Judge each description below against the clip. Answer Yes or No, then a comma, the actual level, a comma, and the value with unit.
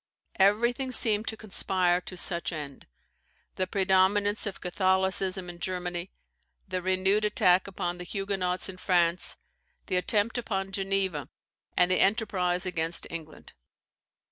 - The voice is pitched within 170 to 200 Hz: Yes, medium, 185 Hz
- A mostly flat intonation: Yes, narrow, 2.0 semitones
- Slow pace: Yes, slow, 125 wpm